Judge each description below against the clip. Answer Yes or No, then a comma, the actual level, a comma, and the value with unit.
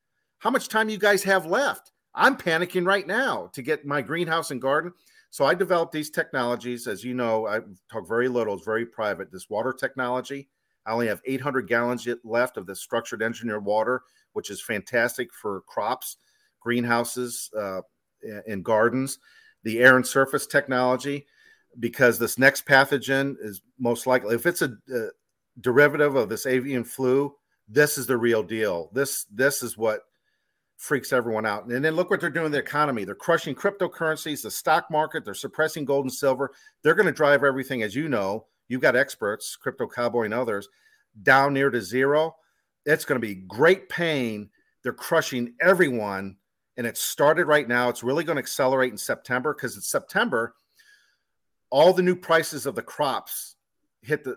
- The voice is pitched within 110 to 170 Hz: Yes, low, 135 Hz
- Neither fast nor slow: Yes, average, 175 wpm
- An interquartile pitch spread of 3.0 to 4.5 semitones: No, average, 4.9 semitones